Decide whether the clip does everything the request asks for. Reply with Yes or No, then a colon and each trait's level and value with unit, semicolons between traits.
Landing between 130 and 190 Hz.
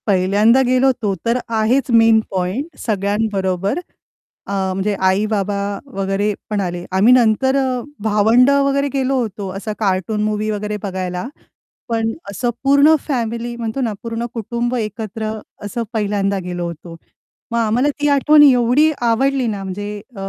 No: high, 220 Hz